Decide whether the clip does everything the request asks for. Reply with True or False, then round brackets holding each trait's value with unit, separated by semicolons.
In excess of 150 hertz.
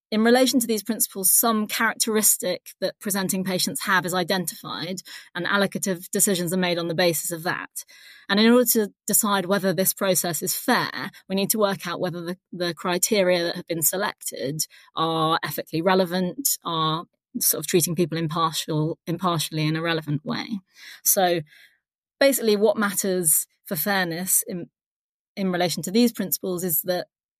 True (185 Hz)